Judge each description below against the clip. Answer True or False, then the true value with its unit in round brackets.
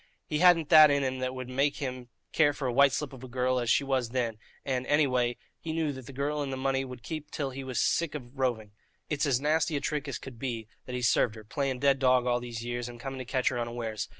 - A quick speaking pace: True (270 wpm)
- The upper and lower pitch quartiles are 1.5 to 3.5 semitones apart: True (2.6 semitones)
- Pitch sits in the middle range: False (130 Hz)